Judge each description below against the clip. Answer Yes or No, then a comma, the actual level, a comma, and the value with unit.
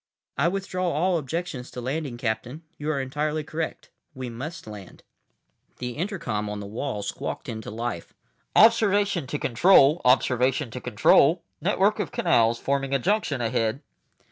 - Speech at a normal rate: Yes, average, 145 wpm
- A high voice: No, medium, 140 Hz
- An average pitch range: No, wide, 6.1 semitones